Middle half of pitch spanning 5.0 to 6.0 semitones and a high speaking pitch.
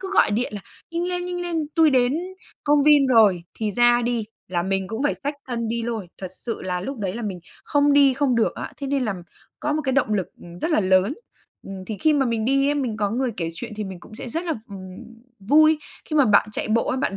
Yes: wide, 5.6 semitones; high, 240 Hz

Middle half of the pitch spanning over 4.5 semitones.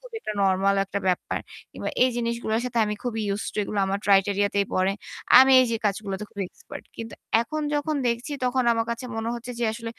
No: average, 3.4 semitones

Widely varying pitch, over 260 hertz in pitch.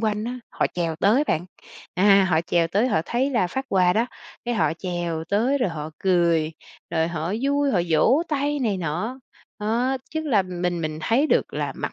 No: wide, 6.6 semitones; high, 195 Hz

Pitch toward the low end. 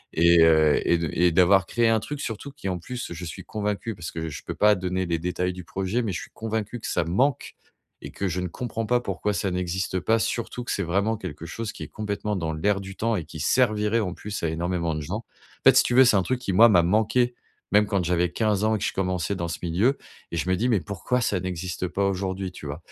Yes: very low, 95 Hz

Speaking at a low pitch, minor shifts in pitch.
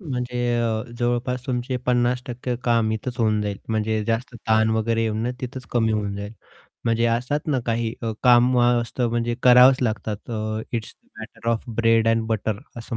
Yes: low, 115 Hz; narrow, 1.7 semitones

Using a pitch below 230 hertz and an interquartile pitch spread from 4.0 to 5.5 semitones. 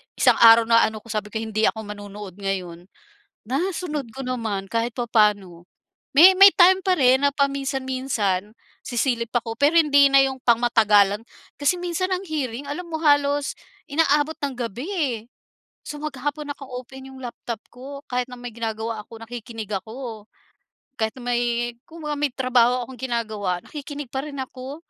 No: very high, 250 Hz; average, 4.3 semitones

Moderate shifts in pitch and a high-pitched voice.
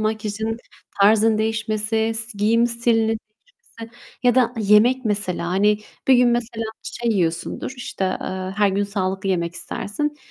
No: narrow, 2.3 semitones; high, 220 Hz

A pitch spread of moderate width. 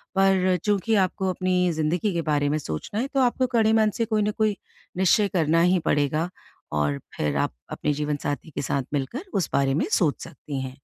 No: wide, 6.1 semitones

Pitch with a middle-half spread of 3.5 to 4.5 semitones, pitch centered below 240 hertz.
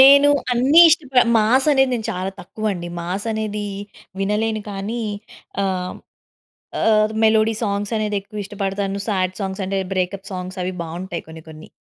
No: average, 2.7 semitones; high, 205 Hz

